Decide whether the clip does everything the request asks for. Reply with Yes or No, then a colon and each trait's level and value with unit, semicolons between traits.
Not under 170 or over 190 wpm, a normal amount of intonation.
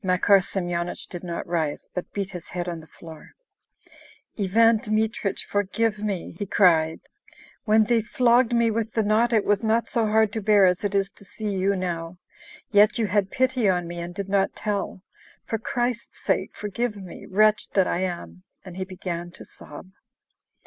Yes: average, 185 wpm; average, 3.4 semitones